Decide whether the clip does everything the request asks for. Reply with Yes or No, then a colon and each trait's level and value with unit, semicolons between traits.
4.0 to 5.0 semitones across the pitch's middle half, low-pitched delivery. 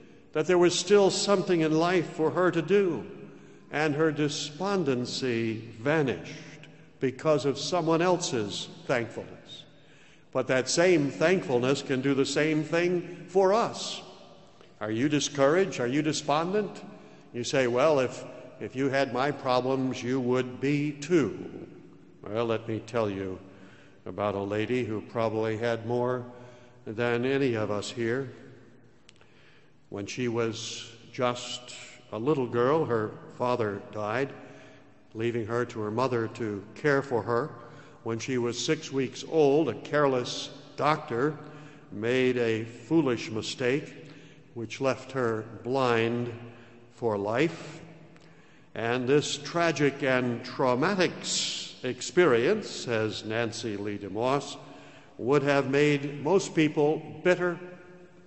Yes: average, 4.6 semitones; low, 130 Hz